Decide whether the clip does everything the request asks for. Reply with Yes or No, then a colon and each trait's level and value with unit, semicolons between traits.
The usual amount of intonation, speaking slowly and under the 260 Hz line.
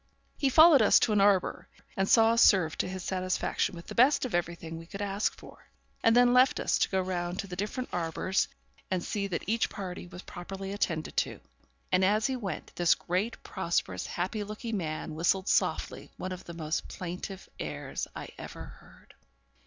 No: average, 3.4 semitones; average, 190 wpm; high, 190 Hz